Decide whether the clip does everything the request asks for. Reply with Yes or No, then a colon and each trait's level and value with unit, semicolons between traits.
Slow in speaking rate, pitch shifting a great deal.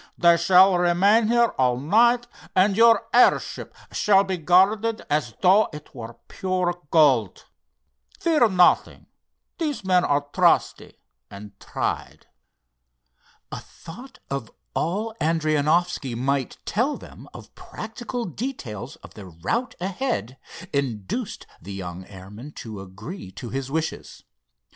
Yes: slow, 120 wpm; wide, 8.9 semitones